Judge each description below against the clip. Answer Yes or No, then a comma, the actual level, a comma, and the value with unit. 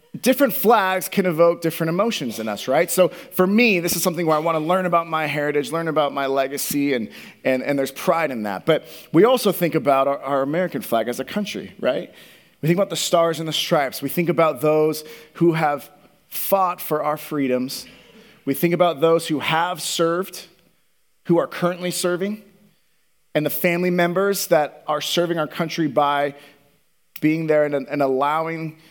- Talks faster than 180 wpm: Yes, average, 190 wpm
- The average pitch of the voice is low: No, medium, 165 Hz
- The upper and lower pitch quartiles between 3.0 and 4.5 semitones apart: Yes, average, 3.5 semitones